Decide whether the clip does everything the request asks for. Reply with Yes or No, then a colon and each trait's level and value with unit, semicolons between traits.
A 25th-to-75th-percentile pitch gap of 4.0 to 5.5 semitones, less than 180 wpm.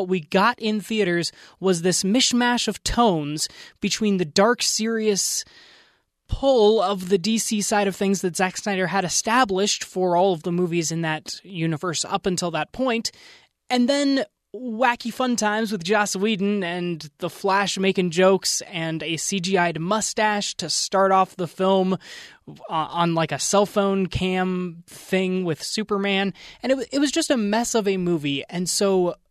No: average, 3.3 semitones; average, 165 wpm